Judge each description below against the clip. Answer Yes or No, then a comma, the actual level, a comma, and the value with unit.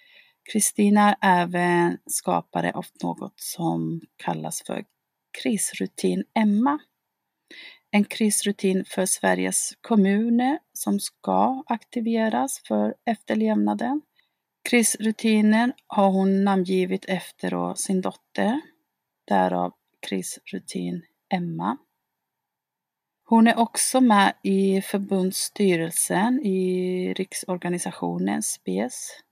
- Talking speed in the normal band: No, slow, 80 wpm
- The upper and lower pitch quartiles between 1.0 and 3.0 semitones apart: No, average, 4.2 semitones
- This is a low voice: No, high, 195 Hz